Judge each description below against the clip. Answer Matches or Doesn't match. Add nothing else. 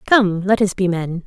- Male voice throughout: Doesn't match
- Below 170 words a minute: Doesn't match